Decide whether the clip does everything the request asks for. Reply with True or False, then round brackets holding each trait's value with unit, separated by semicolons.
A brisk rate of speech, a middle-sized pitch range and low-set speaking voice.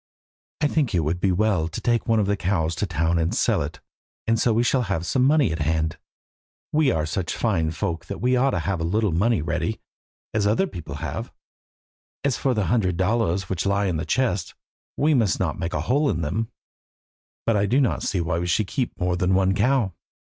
False (220 wpm; 5.7 semitones; 100 Hz)